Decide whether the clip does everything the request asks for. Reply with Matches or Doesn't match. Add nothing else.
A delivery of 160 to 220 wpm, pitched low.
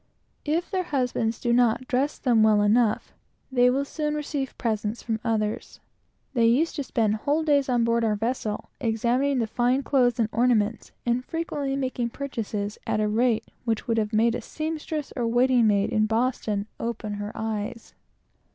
Doesn't match